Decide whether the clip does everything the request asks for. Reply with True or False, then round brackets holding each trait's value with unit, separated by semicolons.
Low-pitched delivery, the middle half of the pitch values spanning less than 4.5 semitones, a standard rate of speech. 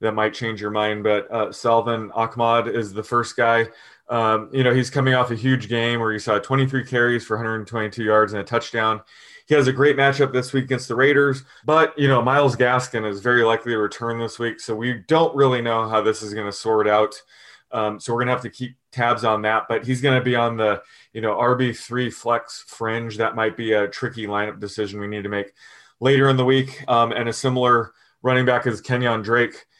False (115 Hz; 2.5 semitones; 230 wpm)